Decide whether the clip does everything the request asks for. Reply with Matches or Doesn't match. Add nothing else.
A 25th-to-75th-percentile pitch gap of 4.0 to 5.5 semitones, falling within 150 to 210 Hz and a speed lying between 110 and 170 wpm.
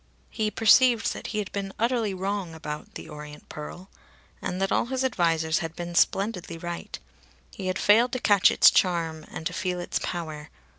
Doesn't match